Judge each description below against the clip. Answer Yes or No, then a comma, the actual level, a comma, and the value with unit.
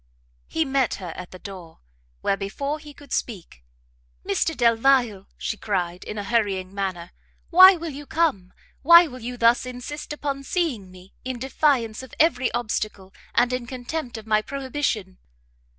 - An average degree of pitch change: No, wide, 5.9 semitones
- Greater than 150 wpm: Yes, average, 160 wpm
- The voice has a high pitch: Yes, high, 240 Hz